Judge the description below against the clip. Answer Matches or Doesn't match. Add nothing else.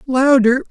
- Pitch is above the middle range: Matches